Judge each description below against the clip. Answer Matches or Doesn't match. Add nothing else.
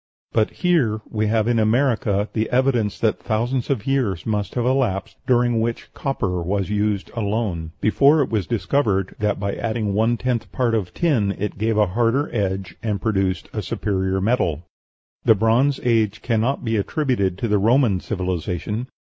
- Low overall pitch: Matches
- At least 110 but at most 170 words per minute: Matches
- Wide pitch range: Doesn't match